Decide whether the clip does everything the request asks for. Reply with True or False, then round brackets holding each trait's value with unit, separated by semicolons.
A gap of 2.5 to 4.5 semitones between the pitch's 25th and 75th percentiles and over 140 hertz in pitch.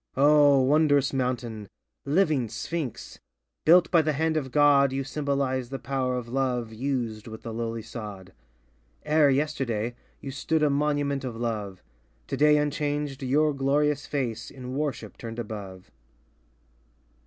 False (3.9 semitones; 135 Hz)